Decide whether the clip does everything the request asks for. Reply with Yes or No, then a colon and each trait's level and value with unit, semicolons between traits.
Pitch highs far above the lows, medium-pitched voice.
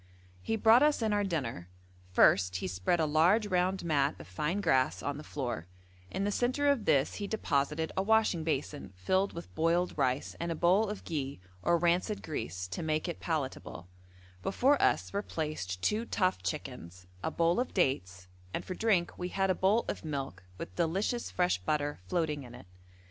Yes: wide, 6.4 semitones; medium, 165 Hz